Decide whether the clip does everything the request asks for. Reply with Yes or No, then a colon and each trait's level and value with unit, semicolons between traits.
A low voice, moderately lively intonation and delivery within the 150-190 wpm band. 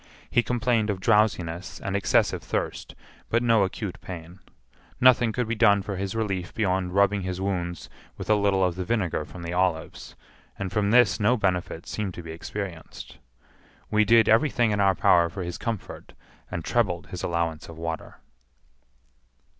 Yes: very low, 95 Hz; average, 3.5 semitones; average, 170 wpm